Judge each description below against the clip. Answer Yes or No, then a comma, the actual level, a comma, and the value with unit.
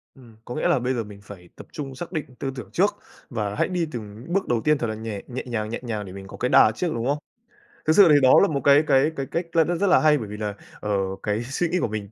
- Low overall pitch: Yes, low, 125 Hz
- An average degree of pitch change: No, wide, 6.1 semitones